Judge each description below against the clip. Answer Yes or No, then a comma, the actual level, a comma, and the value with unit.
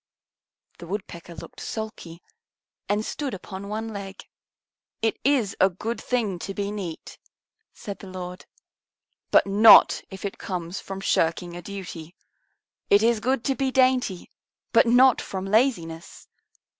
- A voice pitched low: No, high, 200 Hz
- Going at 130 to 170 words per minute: Yes, average, 140 wpm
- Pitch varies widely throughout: No, average, 3.8 semitones